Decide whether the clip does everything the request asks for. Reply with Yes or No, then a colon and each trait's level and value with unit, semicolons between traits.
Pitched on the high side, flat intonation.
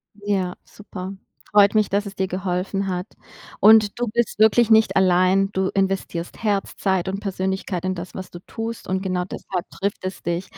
Yes: high, 195 Hz; narrow, 1.9 semitones